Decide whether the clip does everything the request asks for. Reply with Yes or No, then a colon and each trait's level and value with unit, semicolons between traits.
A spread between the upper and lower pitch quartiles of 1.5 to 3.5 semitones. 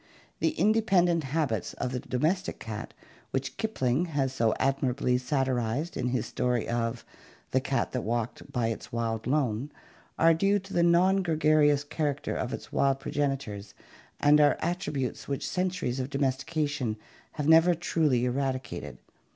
No: average, 4.4 semitones